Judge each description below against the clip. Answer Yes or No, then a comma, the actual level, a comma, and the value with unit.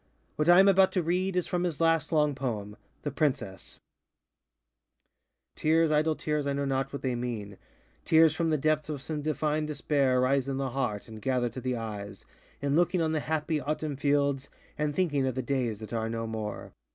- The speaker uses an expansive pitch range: No, average, 3.6 semitones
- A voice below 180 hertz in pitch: Yes, medium, 140 Hz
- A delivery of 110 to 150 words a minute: No, average, 200 wpm